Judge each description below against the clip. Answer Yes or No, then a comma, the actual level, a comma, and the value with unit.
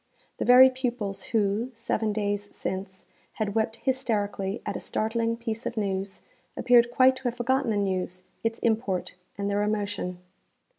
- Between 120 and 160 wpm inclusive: Yes, average, 155 wpm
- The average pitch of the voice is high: Yes, high, 220 Hz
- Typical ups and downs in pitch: Yes, average, 3.0 semitones